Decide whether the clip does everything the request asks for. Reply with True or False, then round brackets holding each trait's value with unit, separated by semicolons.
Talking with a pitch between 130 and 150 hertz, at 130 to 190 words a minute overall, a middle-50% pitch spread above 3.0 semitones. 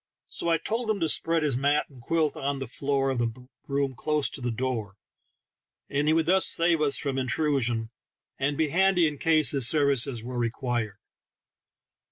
True (140 Hz; 185 wpm; 4.0 semitones)